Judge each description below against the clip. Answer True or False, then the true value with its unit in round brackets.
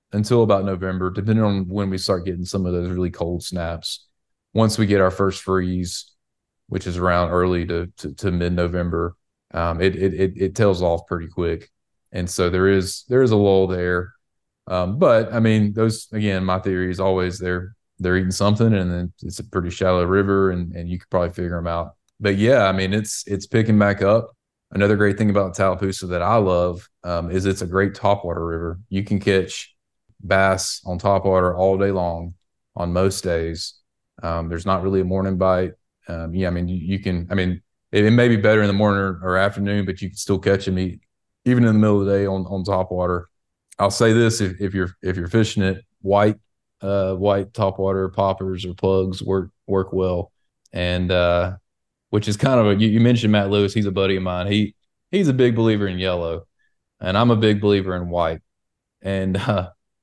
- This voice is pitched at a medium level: False (95 Hz)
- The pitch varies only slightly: True (2.2 semitones)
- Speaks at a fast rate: True (215 wpm)